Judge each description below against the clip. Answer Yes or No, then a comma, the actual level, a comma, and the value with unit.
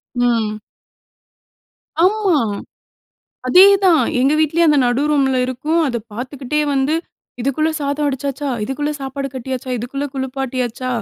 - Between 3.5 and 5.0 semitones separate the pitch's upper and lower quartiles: No, average, 2.9 semitones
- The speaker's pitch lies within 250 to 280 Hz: Yes, very high, 275 Hz